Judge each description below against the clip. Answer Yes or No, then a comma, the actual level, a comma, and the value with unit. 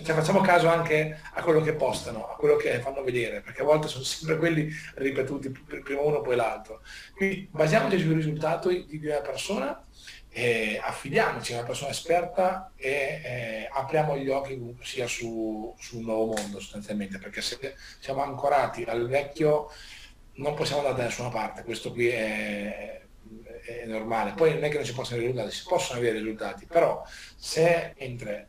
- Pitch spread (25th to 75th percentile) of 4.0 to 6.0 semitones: Yes, average, 5.1 semitones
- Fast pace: Yes, fast, 175 wpm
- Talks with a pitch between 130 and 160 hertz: Yes, low, 135 Hz